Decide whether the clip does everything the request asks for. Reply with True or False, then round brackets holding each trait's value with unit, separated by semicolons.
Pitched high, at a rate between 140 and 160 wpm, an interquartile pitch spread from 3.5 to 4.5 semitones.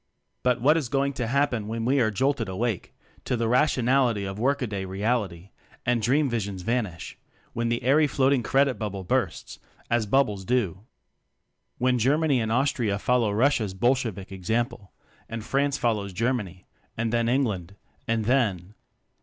False (115 Hz; 155 wpm; 4.1 semitones)